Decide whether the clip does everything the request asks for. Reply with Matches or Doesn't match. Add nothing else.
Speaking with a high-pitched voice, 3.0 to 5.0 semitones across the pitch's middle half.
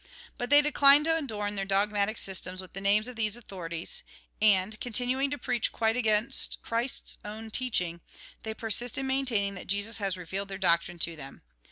Matches